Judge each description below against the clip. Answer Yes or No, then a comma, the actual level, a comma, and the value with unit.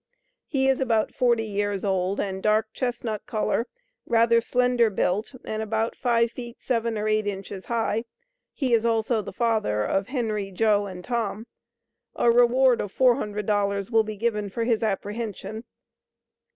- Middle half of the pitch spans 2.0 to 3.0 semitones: Yes, narrow, 2.4 semitones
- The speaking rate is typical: Yes, average, 150 wpm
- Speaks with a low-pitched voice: No, high, 220 Hz